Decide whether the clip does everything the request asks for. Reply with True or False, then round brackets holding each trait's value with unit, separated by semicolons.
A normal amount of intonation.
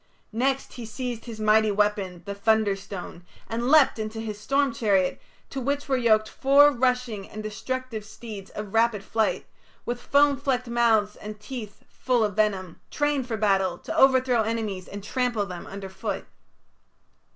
True (3.5 semitones)